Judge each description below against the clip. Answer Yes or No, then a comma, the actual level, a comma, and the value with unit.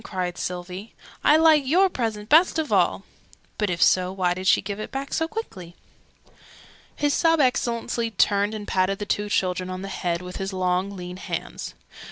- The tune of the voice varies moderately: No, wide, 5.9 semitones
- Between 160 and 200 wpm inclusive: Yes, average, 185 wpm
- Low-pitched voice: No, high, 200 Hz